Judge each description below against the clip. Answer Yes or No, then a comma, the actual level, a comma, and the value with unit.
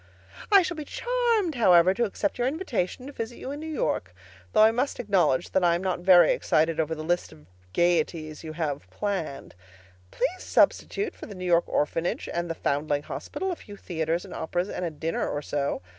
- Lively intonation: Yes, wide, 7.2 semitones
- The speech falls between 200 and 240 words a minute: Yes, fast, 205 wpm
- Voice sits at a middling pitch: Yes, medium, 180 Hz